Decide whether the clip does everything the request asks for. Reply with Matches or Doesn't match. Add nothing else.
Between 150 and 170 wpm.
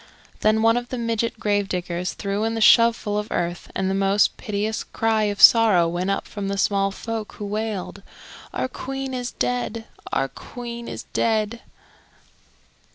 Matches